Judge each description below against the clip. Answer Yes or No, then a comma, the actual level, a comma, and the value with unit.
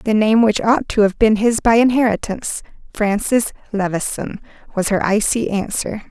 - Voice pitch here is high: Yes, high, 215 Hz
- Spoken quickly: No, average, 145 wpm